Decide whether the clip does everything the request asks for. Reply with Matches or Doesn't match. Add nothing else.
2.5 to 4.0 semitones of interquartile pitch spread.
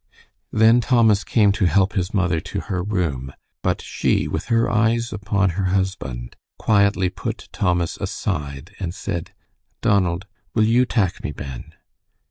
Matches